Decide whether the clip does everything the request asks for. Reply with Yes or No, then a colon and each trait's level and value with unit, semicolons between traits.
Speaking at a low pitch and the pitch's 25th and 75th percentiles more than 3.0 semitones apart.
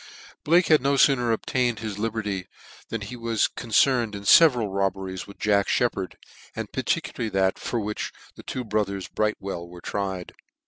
Yes: low, 105 Hz; average, 3.6 semitones